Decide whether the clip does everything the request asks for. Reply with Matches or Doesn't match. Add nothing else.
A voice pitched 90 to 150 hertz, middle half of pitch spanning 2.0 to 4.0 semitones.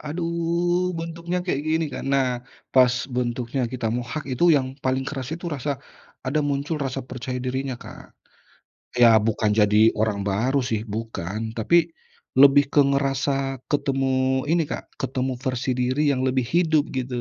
Matches